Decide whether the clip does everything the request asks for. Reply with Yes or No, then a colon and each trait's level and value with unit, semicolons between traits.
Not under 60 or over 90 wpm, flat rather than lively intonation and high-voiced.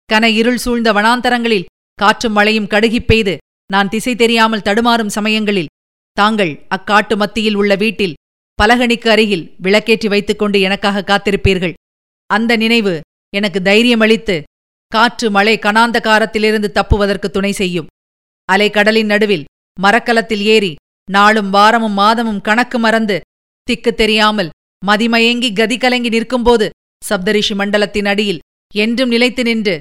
No: average, 110 wpm; narrow, 2.1 semitones; high, 215 Hz